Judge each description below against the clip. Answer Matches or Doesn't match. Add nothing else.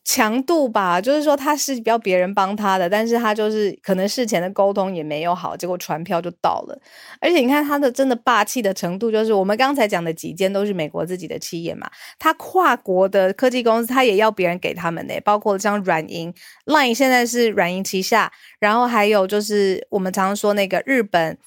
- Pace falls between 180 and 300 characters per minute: Doesn't match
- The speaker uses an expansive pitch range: Doesn't match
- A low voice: Doesn't match